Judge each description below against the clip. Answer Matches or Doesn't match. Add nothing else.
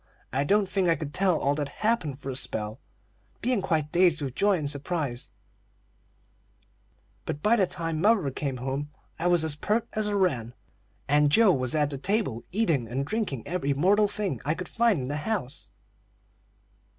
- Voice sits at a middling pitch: Matches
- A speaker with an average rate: Matches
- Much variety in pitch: Matches